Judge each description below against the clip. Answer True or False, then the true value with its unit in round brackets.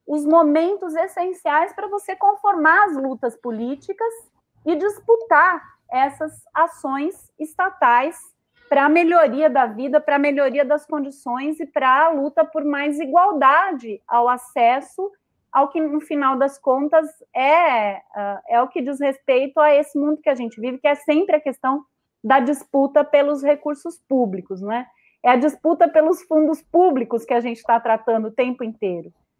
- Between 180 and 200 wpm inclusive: False (155 wpm)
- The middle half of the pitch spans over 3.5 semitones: True (4.0 semitones)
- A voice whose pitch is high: True (295 Hz)